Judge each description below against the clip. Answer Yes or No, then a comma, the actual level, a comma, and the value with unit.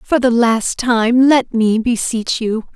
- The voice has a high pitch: Yes, high, 235 Hz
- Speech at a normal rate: Yes, average, 175 wpm